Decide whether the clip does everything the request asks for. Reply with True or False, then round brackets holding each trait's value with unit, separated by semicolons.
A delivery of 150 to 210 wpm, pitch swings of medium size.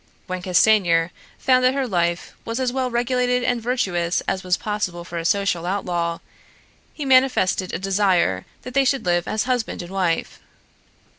False (165 wpm; 6.1 semitones)